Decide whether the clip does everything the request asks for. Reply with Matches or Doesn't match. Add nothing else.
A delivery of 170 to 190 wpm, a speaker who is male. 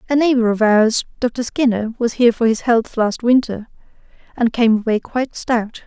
Doesn't match